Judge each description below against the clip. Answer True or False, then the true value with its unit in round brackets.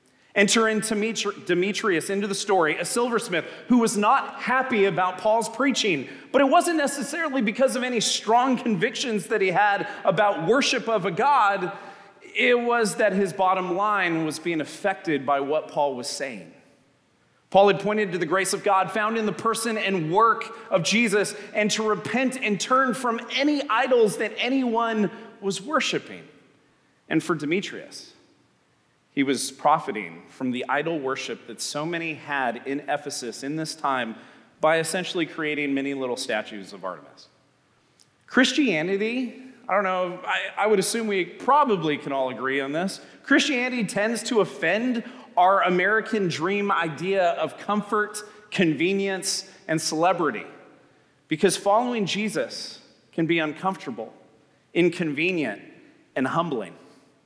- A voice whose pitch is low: False (200 Hz)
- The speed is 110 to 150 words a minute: True (145 wpm)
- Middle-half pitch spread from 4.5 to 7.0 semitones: True (5.2 semitones)